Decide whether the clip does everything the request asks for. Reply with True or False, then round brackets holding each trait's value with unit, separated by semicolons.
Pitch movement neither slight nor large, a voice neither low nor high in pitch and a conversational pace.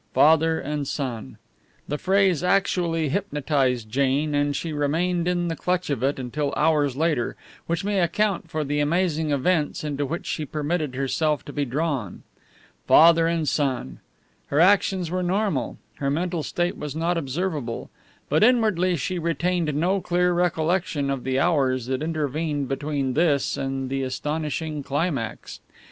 True (3.9 semitones; 155 Hz; 150 wpm)